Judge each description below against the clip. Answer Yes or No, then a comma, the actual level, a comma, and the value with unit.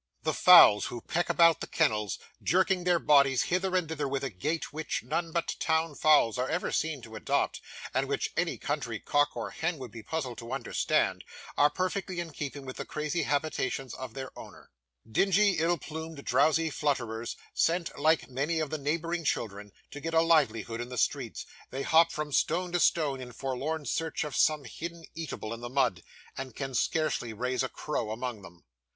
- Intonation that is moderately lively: Yes, average, 4.4 semitones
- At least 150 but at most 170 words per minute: No, average, 190 wpm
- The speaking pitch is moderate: Yes, medium, 145 Hz